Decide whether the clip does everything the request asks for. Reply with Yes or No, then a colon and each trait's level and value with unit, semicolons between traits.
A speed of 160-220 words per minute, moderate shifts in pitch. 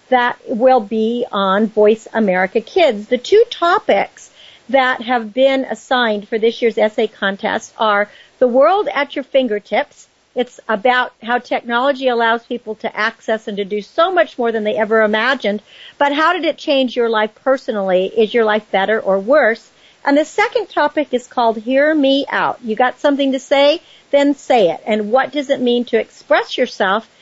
Yes: average, 180 wpm; average, 4.2 semitones